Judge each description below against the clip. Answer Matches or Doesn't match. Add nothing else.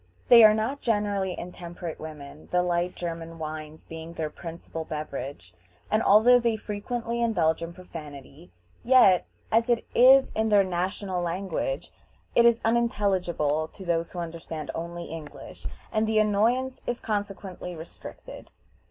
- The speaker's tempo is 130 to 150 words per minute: Matches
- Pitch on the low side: Doesn't match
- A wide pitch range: Doesn't match